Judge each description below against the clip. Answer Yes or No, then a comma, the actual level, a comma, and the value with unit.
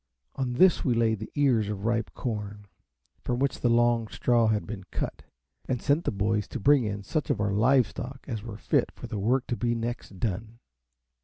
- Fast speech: Yes, fast, 210 wpm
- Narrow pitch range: No, average, 3.0 semitones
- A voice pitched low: Yes, low, 115 Hz